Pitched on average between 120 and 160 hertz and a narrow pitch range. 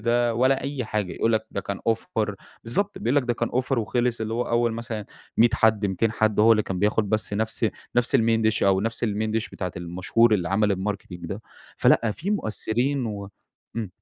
No: low, 110 Hz; narrow, 2.3 semitones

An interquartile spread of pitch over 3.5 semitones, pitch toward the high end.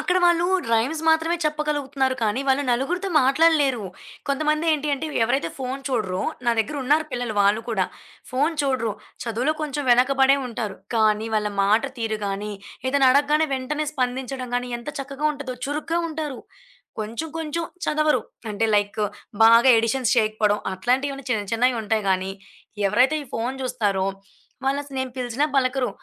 Yes: average, 4.6 semitones; very high, 260 Hz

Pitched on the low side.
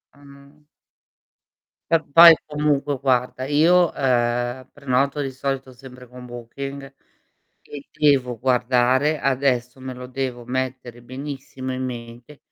Yes: low, 130 Hz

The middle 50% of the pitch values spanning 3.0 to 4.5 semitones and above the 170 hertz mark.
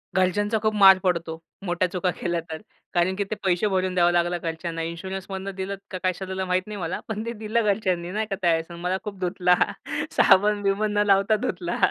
No: narrow, 2.5 semitones; medium, 185 Hz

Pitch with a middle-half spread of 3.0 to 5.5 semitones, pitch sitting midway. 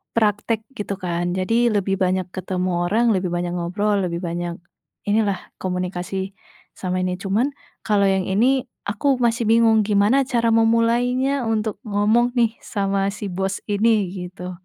No: average, 3.7 semitones; high, 205 Hz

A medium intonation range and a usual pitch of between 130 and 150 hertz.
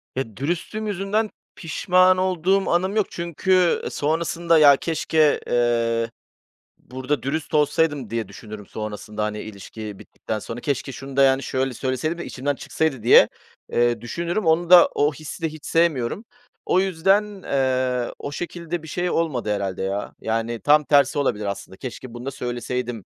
No: wide, 6.1 semitones; medium, 140 Hz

